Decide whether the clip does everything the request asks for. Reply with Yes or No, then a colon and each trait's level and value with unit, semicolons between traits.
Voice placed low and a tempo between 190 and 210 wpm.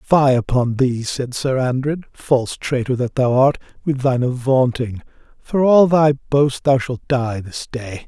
No: low, 130 Hz; average, 170 wpm